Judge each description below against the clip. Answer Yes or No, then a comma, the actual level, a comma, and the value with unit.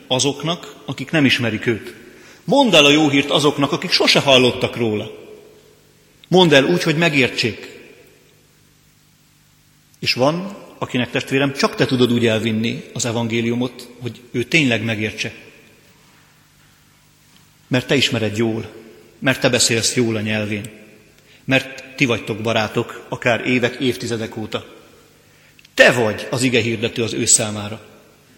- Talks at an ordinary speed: Yes, average, 130 wpm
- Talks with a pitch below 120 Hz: No, low, 125 Hz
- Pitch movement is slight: No, average, 3.8 semitones